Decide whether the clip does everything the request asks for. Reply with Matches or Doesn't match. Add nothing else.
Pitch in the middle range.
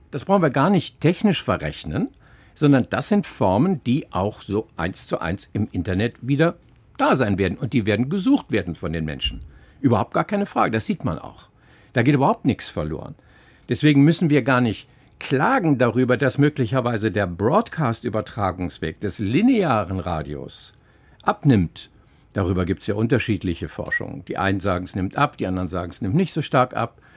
Doesn't match